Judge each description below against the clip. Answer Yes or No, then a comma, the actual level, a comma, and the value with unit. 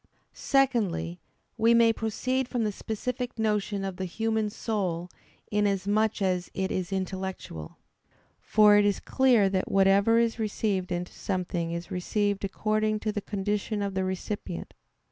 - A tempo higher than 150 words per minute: No, average, 145 wpm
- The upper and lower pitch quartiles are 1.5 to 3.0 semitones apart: Yes, average, 2.7 semitones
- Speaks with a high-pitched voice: Yes, high, 205 Hz